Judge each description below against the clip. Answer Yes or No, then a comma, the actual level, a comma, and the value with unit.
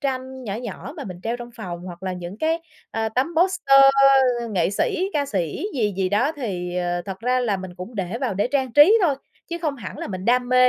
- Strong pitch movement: Yes, wide, 6.5 semitones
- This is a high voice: Yes, high, 235 Hz